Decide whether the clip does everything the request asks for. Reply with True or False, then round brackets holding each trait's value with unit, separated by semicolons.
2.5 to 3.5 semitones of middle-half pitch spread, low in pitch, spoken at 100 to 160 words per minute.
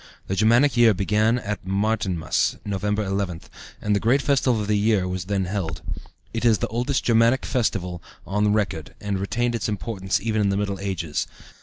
False (2.9 semitones; 105 Hz; 180 wpm)